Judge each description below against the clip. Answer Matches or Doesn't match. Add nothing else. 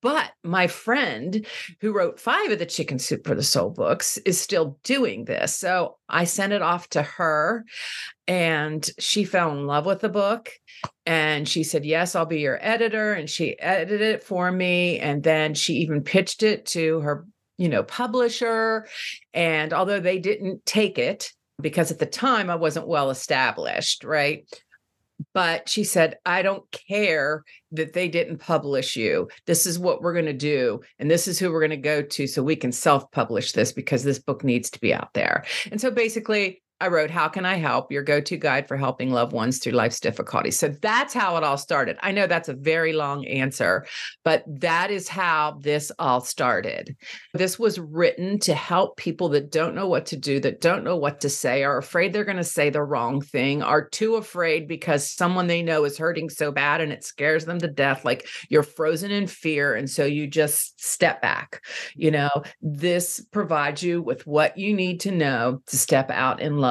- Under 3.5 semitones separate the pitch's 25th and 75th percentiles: Doesn't match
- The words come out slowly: Doesn't match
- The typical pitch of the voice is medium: Matches